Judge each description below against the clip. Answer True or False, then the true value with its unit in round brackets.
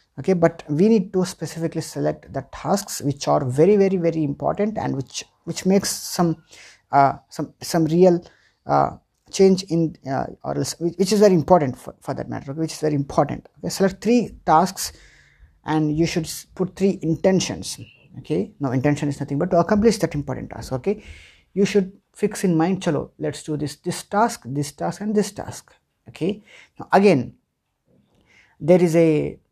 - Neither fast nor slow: True (175 wpm)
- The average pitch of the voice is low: False (165 Hz)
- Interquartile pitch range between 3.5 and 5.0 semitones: True (4.7 semitones)